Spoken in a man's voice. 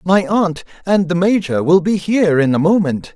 Yes: male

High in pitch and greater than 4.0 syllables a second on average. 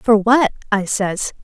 No: high, 215 Hz; 3.5 syllables/s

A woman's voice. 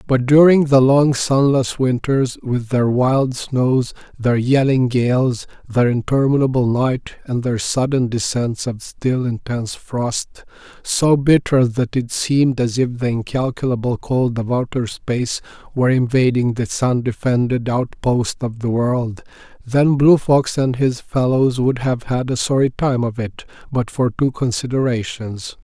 No: male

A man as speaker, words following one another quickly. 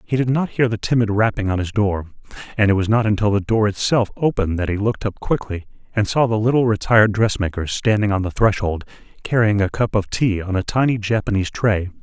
Yes: male; fast, 220 wpm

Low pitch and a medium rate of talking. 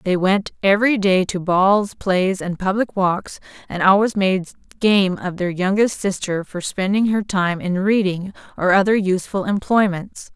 No: high, 190 Hz; average, 160 wpm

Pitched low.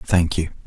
Yes: very low, 85 Hz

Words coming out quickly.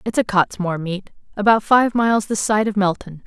No: average, 185 wpm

